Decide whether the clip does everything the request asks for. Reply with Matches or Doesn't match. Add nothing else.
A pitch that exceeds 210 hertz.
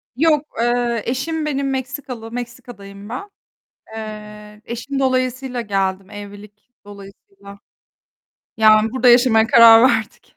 Matches